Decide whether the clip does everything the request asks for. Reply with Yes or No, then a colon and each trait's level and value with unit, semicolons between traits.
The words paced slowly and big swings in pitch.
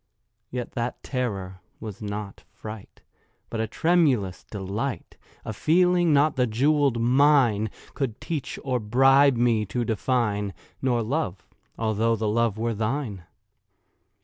No: slow, 120 wpm; average, 4.0 semitones